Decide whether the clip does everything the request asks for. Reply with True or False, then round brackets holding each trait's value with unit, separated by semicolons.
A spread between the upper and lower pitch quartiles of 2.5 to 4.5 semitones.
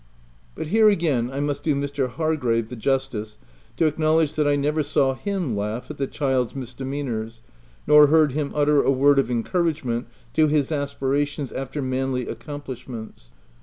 True (2.9 semitones)